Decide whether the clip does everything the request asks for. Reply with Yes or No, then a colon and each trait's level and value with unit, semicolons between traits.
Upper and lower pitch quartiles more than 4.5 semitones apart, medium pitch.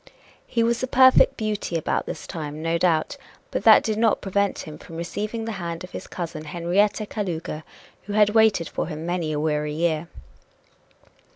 Yes: average, 4.9 semitones; medium, 175 Hz